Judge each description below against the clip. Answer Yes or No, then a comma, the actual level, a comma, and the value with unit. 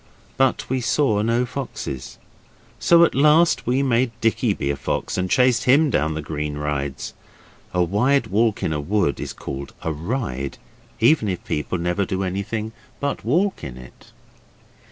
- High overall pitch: No, low, 105 Hz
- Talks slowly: No, average, 165 wpm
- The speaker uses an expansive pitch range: Yes, wide, 8.7 semitones